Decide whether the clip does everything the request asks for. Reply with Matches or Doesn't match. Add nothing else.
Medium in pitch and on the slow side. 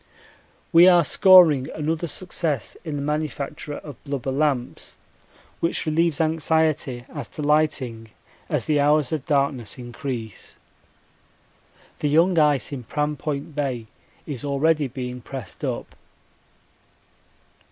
Matches